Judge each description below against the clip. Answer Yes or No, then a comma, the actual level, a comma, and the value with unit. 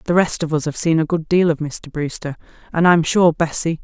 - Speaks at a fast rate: Yes, fast, 250 wpm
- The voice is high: No, medium, 160 Hz